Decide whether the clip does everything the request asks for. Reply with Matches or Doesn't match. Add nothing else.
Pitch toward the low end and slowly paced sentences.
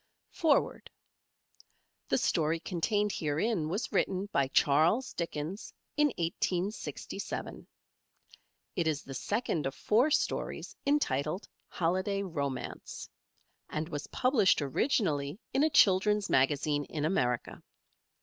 Doesn't match